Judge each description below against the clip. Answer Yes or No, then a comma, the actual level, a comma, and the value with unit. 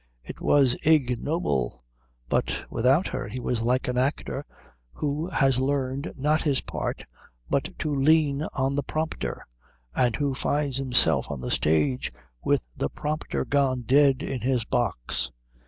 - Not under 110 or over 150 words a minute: Yes, average, 145 wpm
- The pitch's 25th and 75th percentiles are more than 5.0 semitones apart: No, average, 2.9 semitones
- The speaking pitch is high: No, low, 135 Hz